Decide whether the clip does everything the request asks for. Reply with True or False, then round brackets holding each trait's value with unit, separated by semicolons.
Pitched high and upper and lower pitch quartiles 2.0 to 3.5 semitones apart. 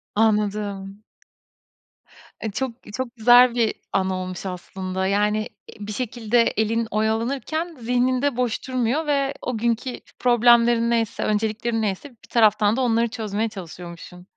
True (225 Hz; 2.8 semitones)